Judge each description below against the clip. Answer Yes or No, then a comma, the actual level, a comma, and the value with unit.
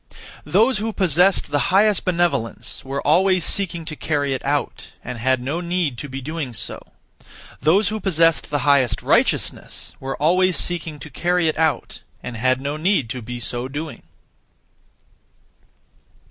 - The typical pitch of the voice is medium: Yes, medium, 155 Hz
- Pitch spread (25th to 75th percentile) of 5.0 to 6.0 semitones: Yes, average, 5.3 semitones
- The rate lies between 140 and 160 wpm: Yes, average, 150 wpm